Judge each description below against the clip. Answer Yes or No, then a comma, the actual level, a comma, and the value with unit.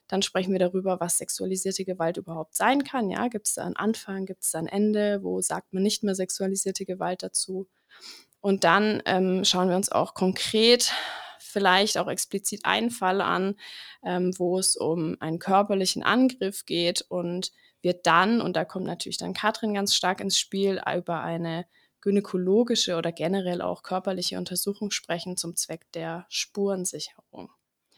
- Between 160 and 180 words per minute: Yes, average, 165 wpm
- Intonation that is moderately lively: No, narrow, 2.2 semitones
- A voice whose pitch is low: No, high, 190 Hz